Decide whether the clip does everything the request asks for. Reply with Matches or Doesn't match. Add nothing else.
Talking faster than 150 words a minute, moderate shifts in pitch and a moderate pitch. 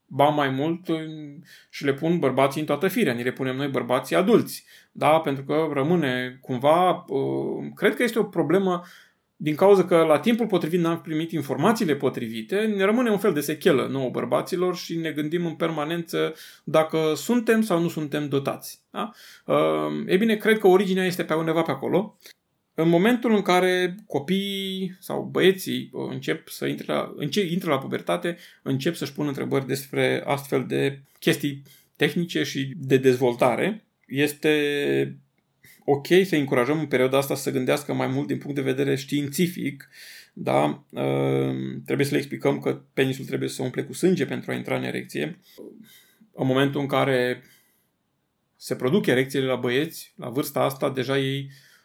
Matches